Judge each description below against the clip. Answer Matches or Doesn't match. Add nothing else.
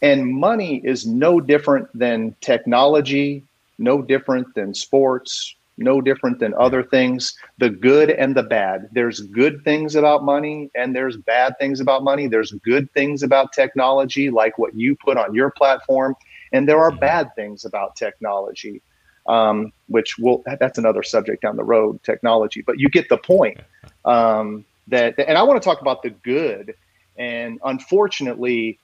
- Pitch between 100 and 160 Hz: Matches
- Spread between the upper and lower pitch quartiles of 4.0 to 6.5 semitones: Doesn't match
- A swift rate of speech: Doesn't match